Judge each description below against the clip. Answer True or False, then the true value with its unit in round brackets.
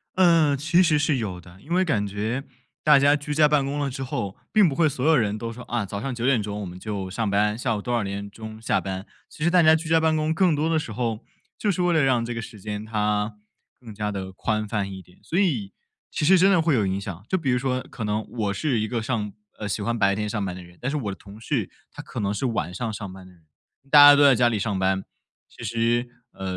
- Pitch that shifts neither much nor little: False (6.1 semitones)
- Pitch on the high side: False (115 Hz)